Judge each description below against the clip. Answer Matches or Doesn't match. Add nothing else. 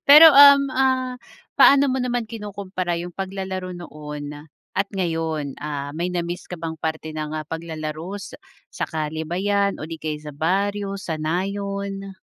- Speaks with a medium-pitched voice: Matches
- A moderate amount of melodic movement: Matches